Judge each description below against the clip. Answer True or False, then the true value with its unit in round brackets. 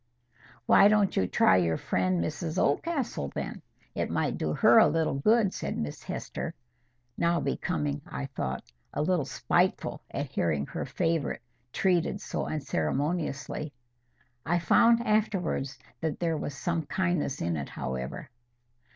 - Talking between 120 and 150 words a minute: True (140 wpm)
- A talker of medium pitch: True (155 Hz)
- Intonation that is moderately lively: False (6.0 semitones)